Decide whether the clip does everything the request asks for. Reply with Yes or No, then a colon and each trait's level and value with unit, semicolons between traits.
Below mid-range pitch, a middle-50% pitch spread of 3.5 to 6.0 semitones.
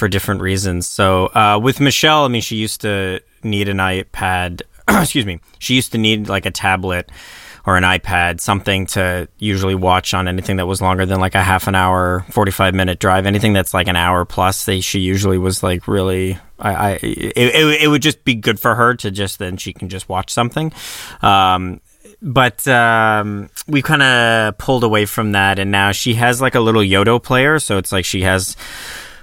Yes: low, 100 Hz; average, 3.9 semitones